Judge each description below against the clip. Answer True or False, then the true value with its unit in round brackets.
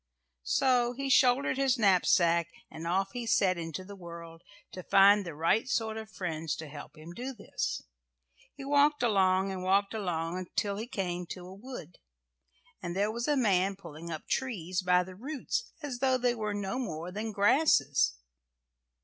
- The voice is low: False (195 Hz)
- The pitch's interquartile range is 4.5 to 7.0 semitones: True (5.6 semitones)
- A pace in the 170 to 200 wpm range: True (175 wpm)